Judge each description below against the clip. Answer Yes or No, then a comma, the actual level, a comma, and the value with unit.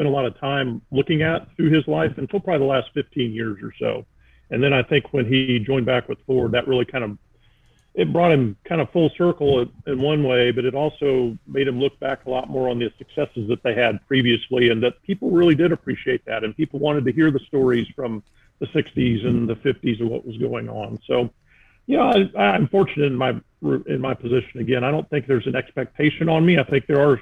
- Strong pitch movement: No, average, 3.4 semitones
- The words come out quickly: Yes, fast, 235 wpm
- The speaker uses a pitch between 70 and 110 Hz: No, low, 130 Hz